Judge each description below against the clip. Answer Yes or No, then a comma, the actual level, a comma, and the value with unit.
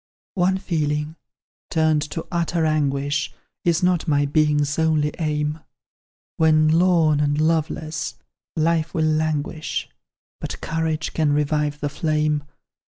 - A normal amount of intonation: No, narrow, 1.5 semitones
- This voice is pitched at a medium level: Yes, medium, 155 Hz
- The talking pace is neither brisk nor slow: No, slow, 115 wpm